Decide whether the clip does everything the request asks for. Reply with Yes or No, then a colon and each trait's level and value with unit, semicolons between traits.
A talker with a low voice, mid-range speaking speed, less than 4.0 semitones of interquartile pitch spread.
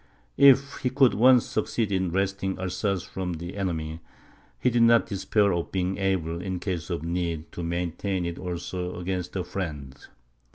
Yes: very low, 95 Hz; average, 165 wpm; narrow, 2.5 semitones